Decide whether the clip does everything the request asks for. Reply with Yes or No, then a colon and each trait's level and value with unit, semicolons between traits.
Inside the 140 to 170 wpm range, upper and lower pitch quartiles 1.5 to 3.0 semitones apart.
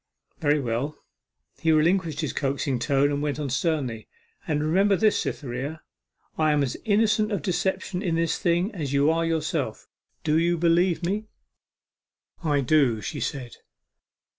No: average, 150 wpm; average, 3.6 semitones